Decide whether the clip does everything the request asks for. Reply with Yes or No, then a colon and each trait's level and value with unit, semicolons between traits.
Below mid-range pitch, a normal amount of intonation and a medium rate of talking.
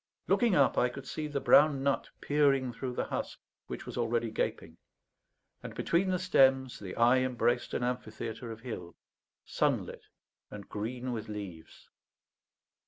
Yes: low, 125 Hz; average, 3.3 semitones; average, 150 wpm